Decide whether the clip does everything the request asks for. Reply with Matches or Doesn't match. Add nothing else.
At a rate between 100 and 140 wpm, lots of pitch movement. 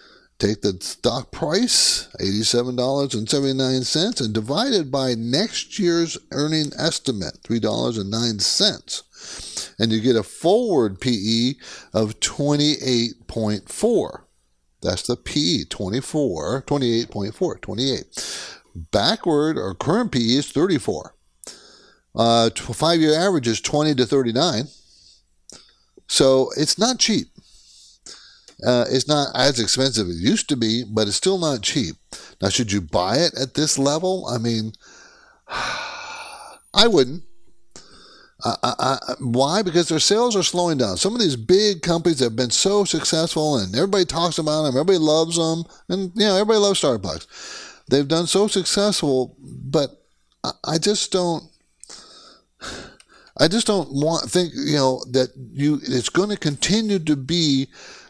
Matches